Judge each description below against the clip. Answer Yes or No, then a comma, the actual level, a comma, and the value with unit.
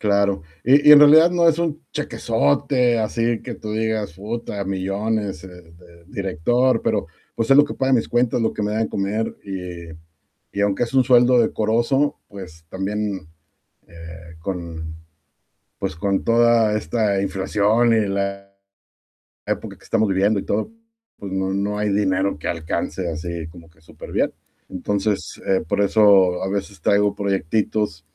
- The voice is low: Yes, low, 100 Hz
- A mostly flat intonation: No, average, 3.2 semitones